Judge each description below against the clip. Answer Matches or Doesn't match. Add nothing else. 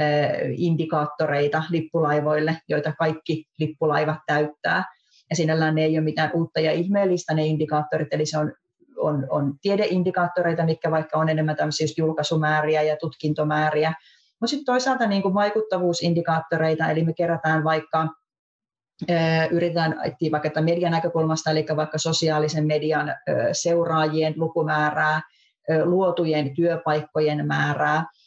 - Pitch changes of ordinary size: Doesn't match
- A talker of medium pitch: Matches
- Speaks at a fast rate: Doesn't match